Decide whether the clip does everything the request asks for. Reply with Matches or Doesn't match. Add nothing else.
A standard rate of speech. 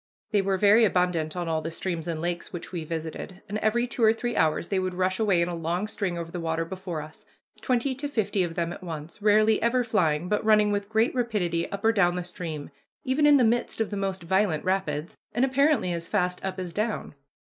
Doesn't match